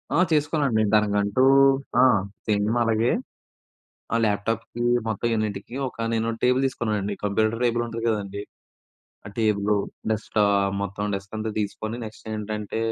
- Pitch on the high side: No, low, 110 Hz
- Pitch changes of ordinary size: No, narrow, 1.9 semitones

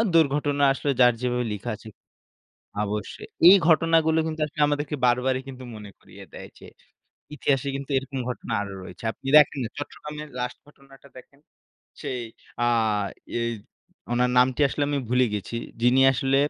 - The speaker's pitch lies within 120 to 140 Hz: Yes, low, 135 Hz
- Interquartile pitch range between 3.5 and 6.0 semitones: No, average, 3.0 semitones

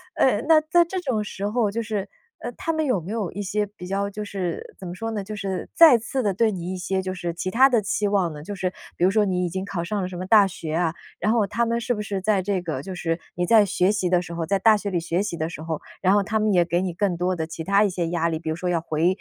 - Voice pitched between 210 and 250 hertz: No, high, 195 Hz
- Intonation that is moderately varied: Yes, average, 3.3 semitones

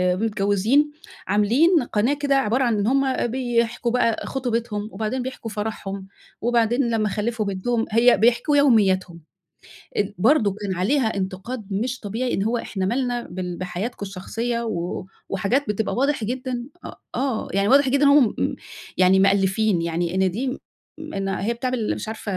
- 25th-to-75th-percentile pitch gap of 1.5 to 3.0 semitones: No, average, 4.2 semitones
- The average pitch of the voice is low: No, high, 225 Hz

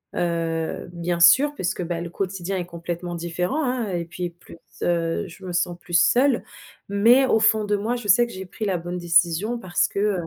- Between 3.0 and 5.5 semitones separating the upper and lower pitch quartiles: Yes, average, 3.6 semitones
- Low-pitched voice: No, medium, 180 Hz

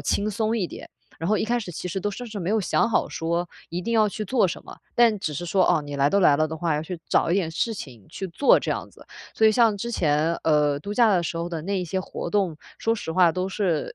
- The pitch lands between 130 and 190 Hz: Yes, medium, 185 Hz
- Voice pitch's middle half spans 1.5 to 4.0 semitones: No, average, 4.6 semitones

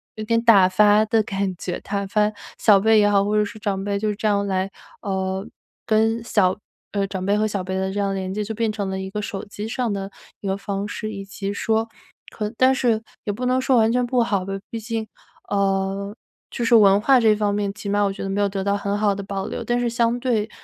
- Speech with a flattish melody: Yes, narrow, 2.1 semitones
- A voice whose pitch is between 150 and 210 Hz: Yes, high, 205 Hz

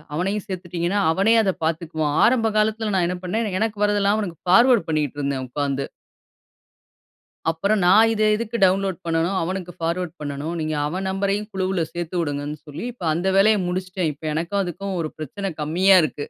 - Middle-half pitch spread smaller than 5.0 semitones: Yes, average, 3.9 semitones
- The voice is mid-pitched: Yes, medium, 180 Hz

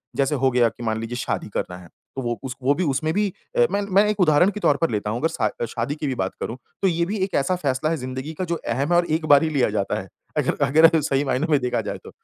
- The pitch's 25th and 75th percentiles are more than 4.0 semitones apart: Yes, average, 5.1 semitones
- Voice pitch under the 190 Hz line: Yes, medium, 140 Hz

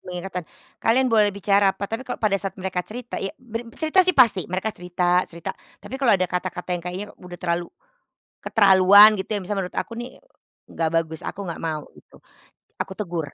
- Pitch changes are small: No, average, 3.5 semitones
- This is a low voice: No, high, 190 Hz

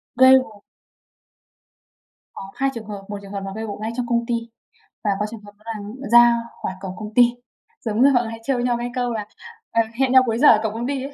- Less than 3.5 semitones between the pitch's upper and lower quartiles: Yes, average, 2.7 semitones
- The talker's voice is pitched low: No, high, 230 Hz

